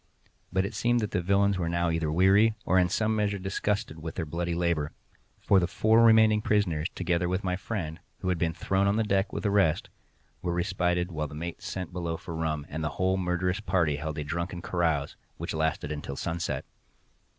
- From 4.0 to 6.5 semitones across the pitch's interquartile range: No, average, 3.2 semitones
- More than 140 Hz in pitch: No, very low, 90 Hz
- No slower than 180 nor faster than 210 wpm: Yes, fast, 205 wpm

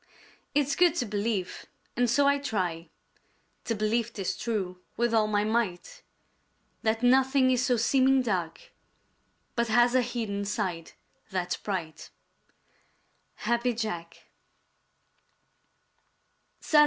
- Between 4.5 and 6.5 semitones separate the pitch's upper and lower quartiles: No, average, 4.0 semitones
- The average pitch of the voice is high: Yes, high, 230 Hz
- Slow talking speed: Yes, slow, 110 wpm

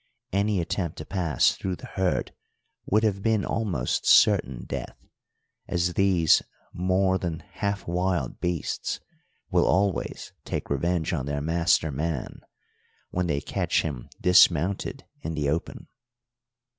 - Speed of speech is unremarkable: No, slow, 130 wpm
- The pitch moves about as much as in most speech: Yes, average, 3.4 semitones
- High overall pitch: No, very low, 90 Hz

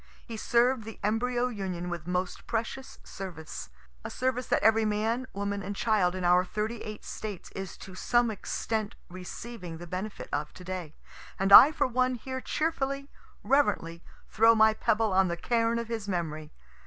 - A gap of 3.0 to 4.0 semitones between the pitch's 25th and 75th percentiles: No, average, 4.4 semitones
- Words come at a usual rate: Yes, average, 170 wpm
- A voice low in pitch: No, high, 215 Hz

